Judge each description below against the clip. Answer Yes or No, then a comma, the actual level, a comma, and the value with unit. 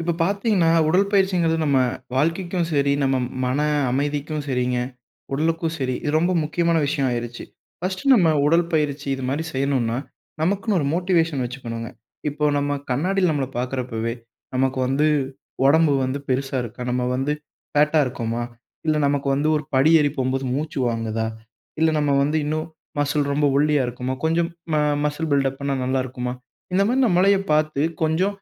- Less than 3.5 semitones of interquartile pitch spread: No, average, 3.8 semitones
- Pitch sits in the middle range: Yes, medium, 145 Hz